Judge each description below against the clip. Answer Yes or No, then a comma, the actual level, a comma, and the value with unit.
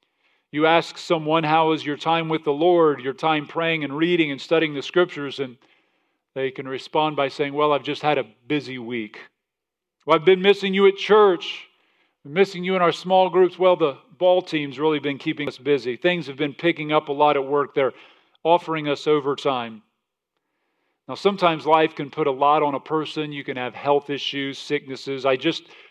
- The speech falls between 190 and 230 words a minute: Yes, average, 200 wpm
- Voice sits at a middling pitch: Yes, medium, 155 Hz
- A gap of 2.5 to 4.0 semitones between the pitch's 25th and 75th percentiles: Yes, average, 3.1 semitones